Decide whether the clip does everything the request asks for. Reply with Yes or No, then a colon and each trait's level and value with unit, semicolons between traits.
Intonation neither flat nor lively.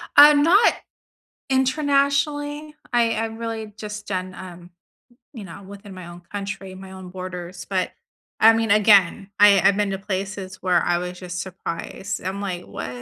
Yes: average, 3.4 semitones